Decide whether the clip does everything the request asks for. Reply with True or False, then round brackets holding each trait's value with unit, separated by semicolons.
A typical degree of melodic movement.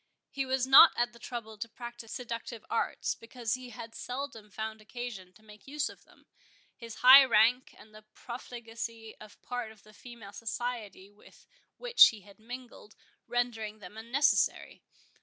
False (2.3 semitones)